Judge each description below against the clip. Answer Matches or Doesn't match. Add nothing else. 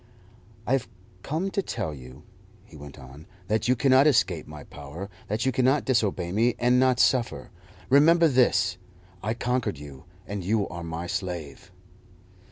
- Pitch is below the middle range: Matches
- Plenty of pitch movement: Matches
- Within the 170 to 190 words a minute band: Doesn't match